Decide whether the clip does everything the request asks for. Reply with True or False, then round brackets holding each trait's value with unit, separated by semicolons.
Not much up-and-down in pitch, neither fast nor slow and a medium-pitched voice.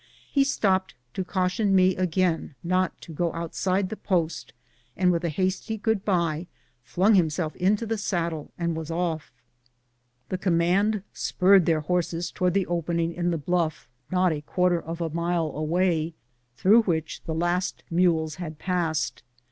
True (2.2 semitones; 155 wpm; 175 Hz)